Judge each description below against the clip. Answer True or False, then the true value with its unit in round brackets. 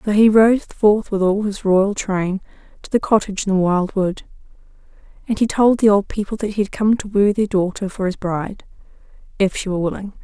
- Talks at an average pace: False (210 wpm)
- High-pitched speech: True (200 Hz)